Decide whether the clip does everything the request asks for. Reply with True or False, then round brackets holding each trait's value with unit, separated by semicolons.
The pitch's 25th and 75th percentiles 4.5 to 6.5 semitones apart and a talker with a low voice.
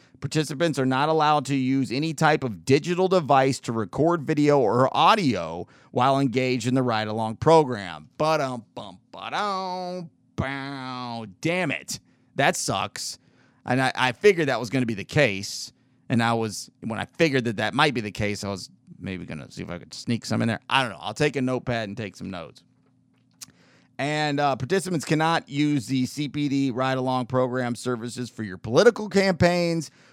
False (3.9 semitones; 130 Hz)